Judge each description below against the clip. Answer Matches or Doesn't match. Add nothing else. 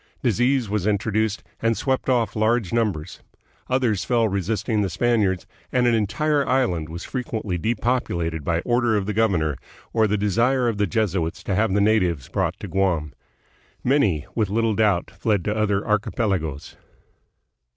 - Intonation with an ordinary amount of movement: Matches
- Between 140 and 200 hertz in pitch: Doesn't match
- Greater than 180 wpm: Doesn't match